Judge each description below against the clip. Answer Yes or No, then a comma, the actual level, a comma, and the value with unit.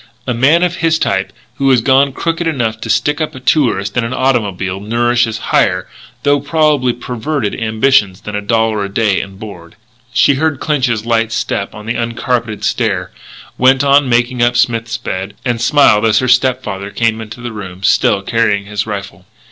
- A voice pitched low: Yes, low, 115 Hz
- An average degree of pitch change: Yes, average, 3.9 semitones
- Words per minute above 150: Yes, average, 185 wpm